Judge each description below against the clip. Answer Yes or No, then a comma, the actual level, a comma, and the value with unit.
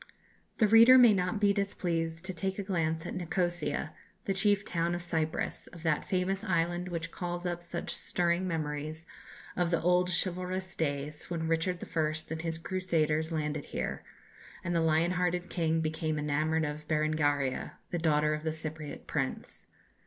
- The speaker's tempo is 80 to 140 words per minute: No, average, 165 wpm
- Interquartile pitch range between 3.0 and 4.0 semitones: No, narrow, 2.5 semitones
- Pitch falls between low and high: Yes, medium, 170 Hz